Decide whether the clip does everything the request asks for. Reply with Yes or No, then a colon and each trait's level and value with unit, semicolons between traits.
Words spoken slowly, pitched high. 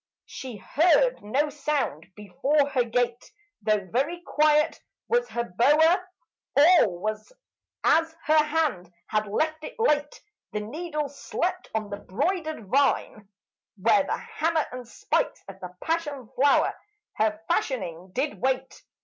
Yes: slow, 130 wpm; very high, 275 Hz